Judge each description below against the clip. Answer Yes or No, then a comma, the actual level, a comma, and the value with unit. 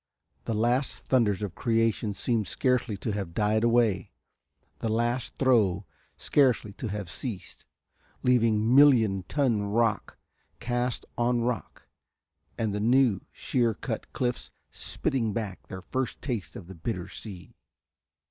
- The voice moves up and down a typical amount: Yes, average, 3.2 semitones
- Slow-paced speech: Yes, slow, 130 wpm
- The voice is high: No, low, 115 Hz